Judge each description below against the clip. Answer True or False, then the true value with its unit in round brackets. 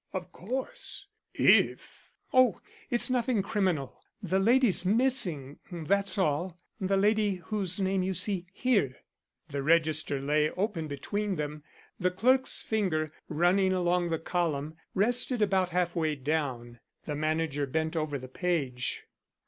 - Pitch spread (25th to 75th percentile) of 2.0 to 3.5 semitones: False (4.6 semitones)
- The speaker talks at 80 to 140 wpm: True (135 wpm)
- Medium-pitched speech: True (180 Hz)